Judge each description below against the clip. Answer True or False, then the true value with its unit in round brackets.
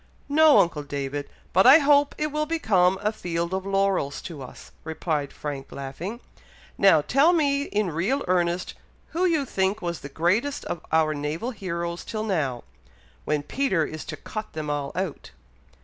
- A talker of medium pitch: True (180 Hz)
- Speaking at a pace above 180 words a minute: False (165 wpm)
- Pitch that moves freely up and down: True (7.5 semitones)